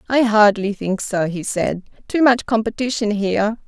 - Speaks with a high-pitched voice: Yes, high, 215 Hz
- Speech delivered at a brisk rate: No, average, 165 wpm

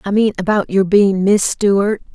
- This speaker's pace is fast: No, average, 195 wpm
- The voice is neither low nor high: No, high, 200 Hz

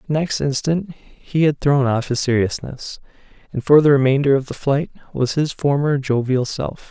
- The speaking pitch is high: No, medium, 140 Hz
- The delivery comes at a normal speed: Yes, average, 175 wpm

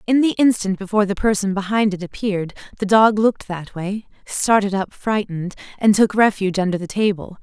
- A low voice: No, high, 200 Hz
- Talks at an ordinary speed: Yes, average, 170 wpm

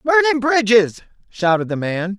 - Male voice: Yes, male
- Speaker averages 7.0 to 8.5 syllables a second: Yes, 7.2 syllables/s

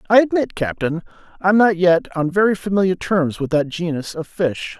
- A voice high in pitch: No, medium, 180 Hz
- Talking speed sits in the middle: Yes, average, 190 wpm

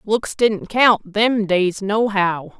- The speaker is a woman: Yes, female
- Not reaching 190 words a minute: Yes, average, 140 wpm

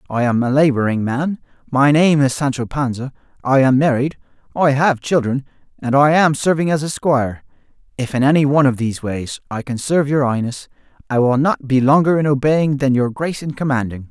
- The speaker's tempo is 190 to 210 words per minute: Yes, average, 200 wpm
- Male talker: Yes, male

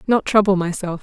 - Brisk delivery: No, average, 175 wpm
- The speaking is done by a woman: Yes, female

